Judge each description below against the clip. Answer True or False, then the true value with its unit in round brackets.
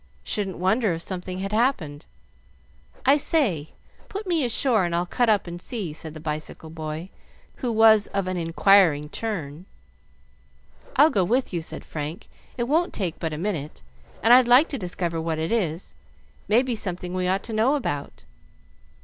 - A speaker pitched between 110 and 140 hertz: False (185 Hz)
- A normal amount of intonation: False (6.1 semitones)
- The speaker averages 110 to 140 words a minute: False (175 wpm)